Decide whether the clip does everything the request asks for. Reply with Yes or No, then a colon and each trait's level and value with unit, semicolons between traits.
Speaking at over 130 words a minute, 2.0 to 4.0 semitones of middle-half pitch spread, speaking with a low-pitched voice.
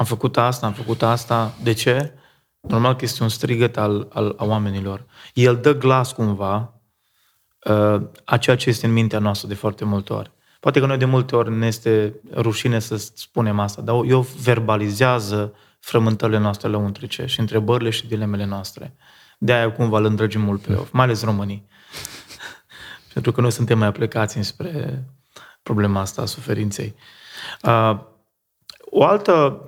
Yes: average, 165 wpm; average, 2.7 semitones; low, 115 Hz